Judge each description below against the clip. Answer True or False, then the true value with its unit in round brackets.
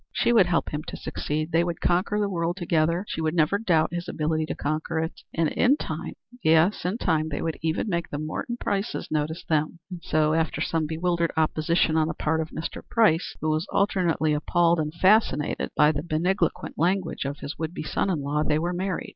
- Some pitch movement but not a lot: False (2.2 semitones)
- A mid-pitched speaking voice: True (165 Hz)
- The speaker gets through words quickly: True (215 wpm)